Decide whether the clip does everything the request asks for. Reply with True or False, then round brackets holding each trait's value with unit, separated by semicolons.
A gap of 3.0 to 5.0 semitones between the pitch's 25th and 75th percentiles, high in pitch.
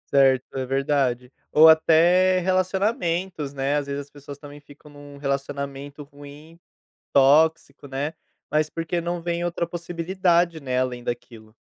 False (3.6 semitones; 145 Hz)